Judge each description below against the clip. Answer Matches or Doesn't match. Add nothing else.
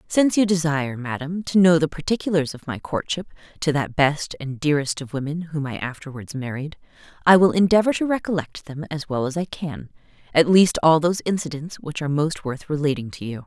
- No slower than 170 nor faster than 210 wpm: Matches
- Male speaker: Doesn't match